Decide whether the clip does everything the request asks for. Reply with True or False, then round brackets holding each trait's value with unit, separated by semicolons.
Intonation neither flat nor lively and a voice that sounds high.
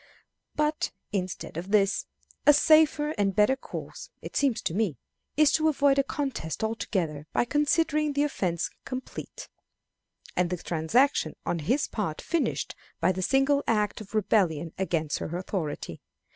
False (8.3 semitones; 215 Hz)